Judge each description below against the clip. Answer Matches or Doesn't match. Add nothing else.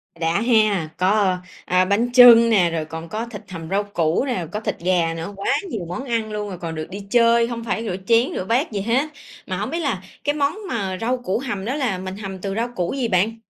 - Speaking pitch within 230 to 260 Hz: Doesn't match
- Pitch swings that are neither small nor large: Matches